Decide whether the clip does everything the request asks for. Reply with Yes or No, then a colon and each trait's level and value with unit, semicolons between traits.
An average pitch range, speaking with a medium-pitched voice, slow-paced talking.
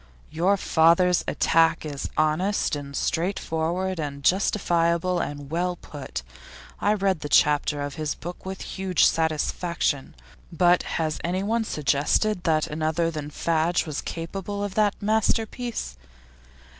Yes: average, 3.5 semitones; medium, 170 Hz; slow, 125 wpm